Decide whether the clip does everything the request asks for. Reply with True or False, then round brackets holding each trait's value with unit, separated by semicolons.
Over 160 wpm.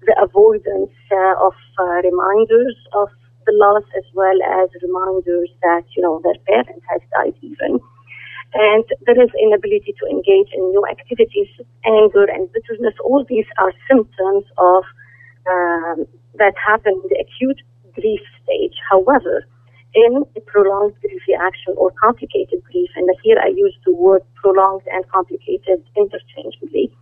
False (145 wpm)